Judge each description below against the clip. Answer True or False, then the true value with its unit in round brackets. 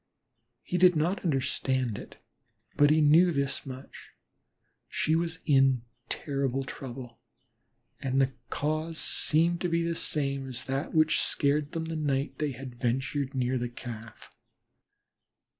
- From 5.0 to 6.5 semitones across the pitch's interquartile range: False (3.1 semitones)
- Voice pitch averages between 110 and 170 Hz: True (140 Hz)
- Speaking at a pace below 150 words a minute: True (140 wpm)